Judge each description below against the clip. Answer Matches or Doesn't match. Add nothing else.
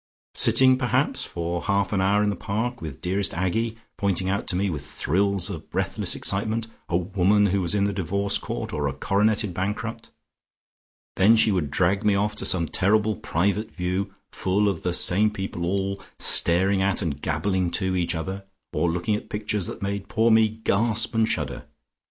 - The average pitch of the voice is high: Doesn't match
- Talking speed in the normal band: Matches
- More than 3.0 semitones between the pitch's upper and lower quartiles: Doesn't match